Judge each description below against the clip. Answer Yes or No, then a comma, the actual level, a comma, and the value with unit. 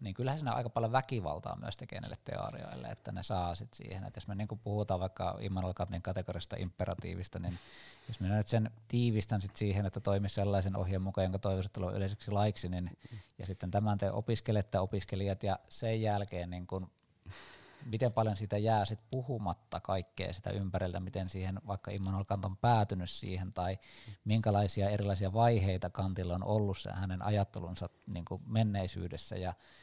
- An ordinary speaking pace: No, fast, 170 wpm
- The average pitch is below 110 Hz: Yes, low, 100 Hz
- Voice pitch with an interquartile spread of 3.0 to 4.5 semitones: No, narrow, 2.6 semitones